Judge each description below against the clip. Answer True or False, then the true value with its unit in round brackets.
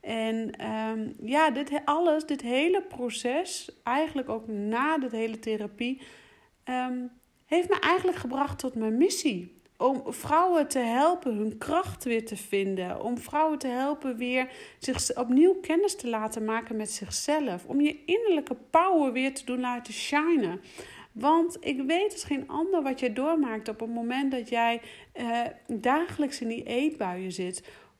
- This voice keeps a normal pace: True (155 wpm)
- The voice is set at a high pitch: True (260 Hz)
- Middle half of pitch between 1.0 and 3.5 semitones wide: False (5.2 semitones)